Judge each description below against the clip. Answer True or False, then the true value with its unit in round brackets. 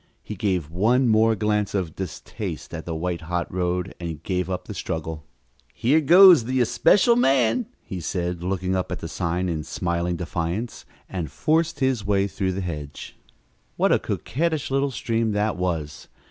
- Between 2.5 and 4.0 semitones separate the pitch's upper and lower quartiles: False (5.3 semitones)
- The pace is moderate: True (170 wpm)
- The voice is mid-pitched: False (95 Hz)